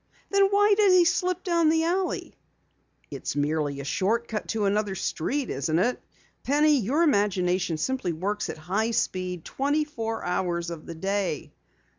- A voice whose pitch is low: No, high, 210 Hz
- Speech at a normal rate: Yes, average, 160 wpm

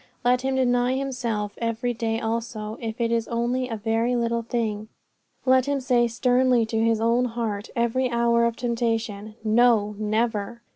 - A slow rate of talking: No, average, 165 wpm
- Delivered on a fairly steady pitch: Yes, narrow, 1.7 semitones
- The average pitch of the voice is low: No, high, 235 Hz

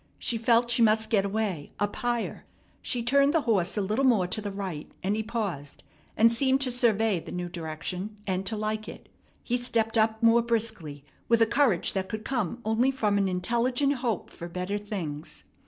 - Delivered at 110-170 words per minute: No, average, 195 wpm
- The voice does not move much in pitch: No, average, 3.7 semitones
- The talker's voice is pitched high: Yes, high, 220 Hz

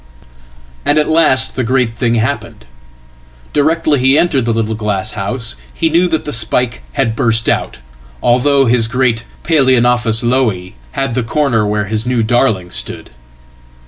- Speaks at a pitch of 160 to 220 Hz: No, low, 120 Hz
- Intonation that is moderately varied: Yes, average, 3.3 semitones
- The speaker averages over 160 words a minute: No, average, 145 wpm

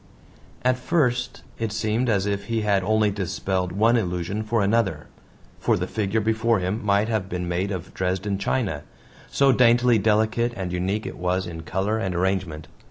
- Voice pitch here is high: No, low, 100 Hz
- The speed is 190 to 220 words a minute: No, average, 170 wpm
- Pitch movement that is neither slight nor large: Yes, average, 3.2 semitones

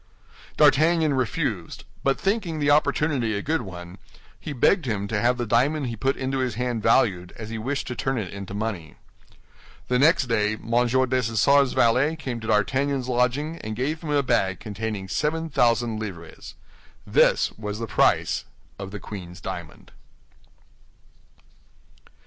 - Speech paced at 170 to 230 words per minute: No, average, 155 wpm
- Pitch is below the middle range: Yes, low, 120 Hz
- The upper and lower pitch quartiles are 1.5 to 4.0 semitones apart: No, average, 4.9 semitones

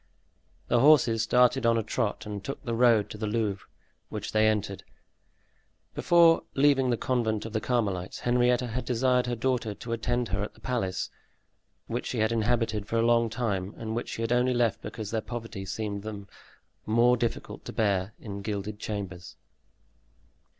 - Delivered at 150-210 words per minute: Yes, average, 180 wpm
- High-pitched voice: No, low, 115 Hz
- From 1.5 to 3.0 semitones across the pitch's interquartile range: Yes, narrow, 2.6 semitones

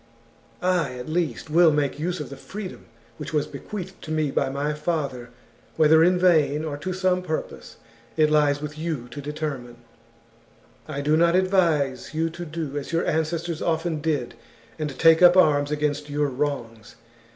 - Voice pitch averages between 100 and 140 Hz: No, medium, 155 Hz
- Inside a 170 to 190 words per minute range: Yes, average, 175 wpm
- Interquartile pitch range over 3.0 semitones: No, average, 2.7 semitones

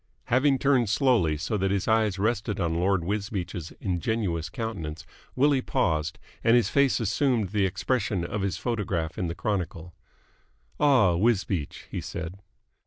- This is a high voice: No, low, 100 Hz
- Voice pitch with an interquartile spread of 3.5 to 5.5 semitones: Yes, average, 5.0 semitones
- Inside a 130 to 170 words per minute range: Yes, average, 145 wpm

